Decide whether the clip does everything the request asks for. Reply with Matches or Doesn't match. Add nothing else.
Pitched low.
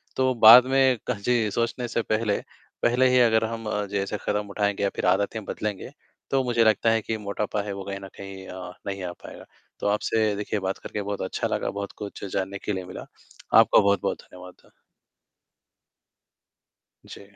Matches